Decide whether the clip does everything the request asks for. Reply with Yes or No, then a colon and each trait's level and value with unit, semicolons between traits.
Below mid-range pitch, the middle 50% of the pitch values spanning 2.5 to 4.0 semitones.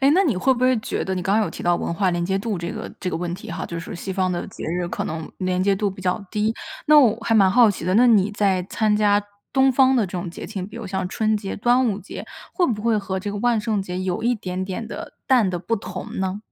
No: high, 205 Hz; average, 3.6 semitones